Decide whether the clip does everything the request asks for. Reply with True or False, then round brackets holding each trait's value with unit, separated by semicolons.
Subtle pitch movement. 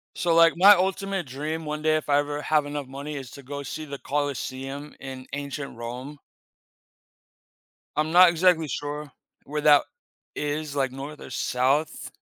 True (2.0 semitones)